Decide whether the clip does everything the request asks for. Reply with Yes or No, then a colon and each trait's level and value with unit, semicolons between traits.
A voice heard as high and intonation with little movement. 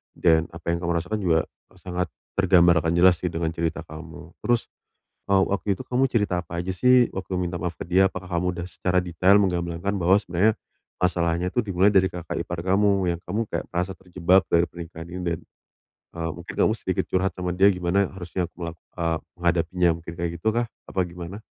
No: very low, 90 Hz; narrow, 2.0 semitones